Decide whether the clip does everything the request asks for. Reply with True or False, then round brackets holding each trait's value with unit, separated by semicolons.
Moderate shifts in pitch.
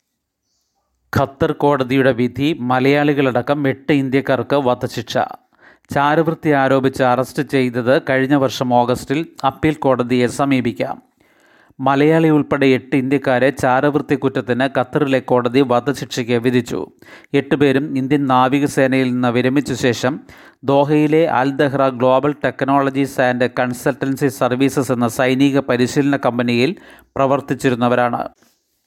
False (2.3 semitones)